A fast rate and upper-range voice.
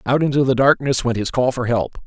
No: fast, 260 wpm; low, 125 Hz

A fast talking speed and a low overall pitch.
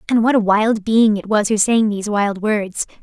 No: fast, 240 wpm; high, 210 Hz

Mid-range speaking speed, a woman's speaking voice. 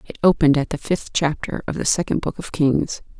No: fast, 225 wpm; female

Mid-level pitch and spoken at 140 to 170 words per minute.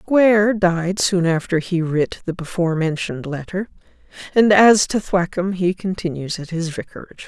Yes: medium, 180 Hz; average, 155 wpm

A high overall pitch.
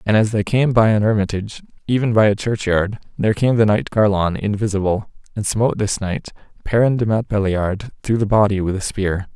No: low, 105 Hz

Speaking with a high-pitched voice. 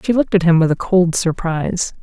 No: medium, 175 Hz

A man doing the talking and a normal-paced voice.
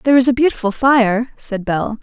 No: female; average, 180 wpm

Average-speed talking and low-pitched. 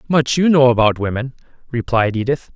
Yes: average, 165 wpm; low, 125 Hz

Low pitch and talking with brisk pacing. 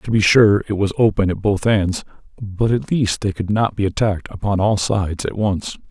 Yes: low, 100 Hz; fast, 225 wpm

